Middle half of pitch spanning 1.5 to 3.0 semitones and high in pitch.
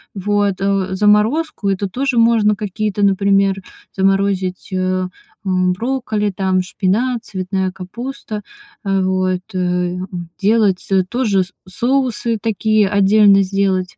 Yes: narrow, 2.4 semitones; high, 195 Hz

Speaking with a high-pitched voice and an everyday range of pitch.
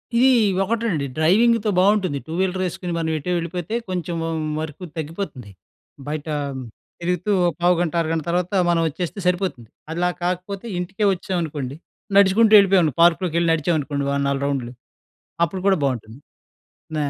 No: medium, 175 Hz; average, 3.6 semitones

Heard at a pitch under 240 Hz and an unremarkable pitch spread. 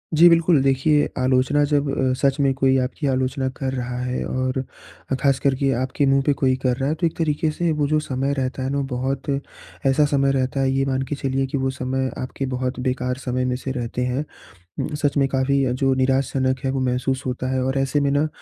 No: low, 135 Hz; narrow, 1.4 semitones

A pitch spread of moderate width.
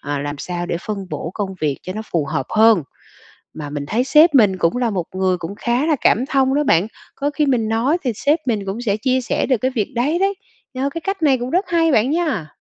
No: wide, 7.0 semitones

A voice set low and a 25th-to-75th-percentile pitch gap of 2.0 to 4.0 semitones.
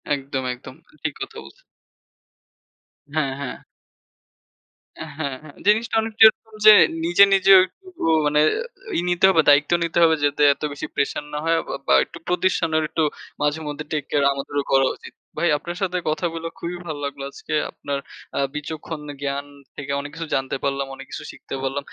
No: medium, 150 Hz; average, 3.5 semitones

